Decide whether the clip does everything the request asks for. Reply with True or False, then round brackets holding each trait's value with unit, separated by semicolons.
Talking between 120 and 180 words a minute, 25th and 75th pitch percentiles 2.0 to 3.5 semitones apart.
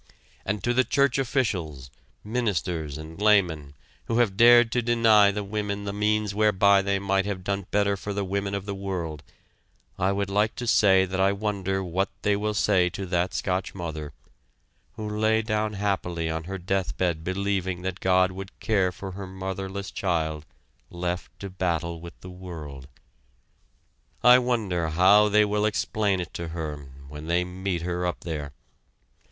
True (170 wpm; 2.9 semitones)